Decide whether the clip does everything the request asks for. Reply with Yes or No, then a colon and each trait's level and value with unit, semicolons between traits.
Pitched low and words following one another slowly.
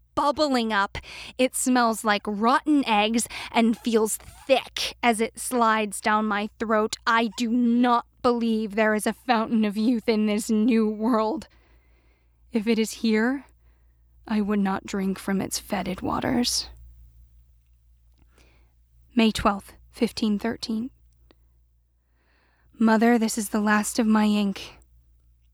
No: high, 215 Hz; slow, 125 wpm